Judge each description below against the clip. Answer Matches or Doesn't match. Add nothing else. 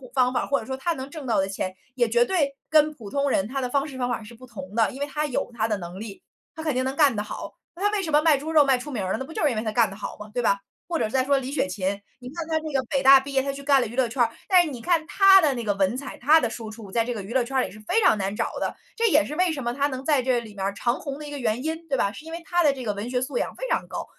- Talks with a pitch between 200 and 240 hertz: Doesn't match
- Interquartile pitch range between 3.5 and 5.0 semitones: Matches